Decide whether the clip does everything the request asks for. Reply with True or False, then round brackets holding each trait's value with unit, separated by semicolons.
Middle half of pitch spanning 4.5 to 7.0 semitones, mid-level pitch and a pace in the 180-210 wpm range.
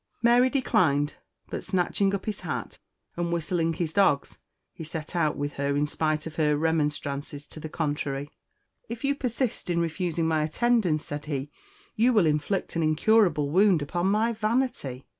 False (5.3 semitones; 165 Hz; 165 wpm)